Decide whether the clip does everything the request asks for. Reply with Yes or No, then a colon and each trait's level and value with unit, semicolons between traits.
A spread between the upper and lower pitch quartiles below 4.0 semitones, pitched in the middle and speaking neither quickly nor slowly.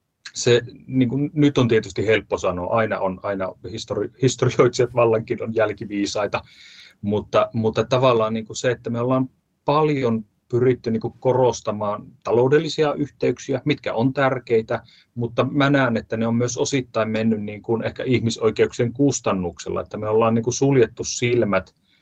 No: average, 2.8 semitones; low, 120 Hz; average, 145 wpm